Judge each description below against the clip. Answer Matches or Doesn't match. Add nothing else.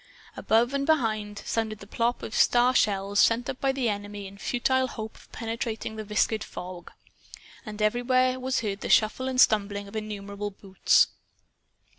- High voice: Matches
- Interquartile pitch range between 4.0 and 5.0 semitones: Doesn't match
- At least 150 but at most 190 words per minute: Matches